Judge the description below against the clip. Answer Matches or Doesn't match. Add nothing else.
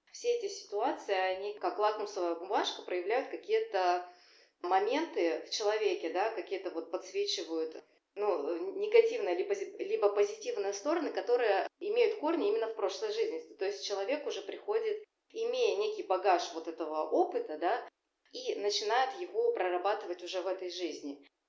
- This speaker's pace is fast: Doesn't match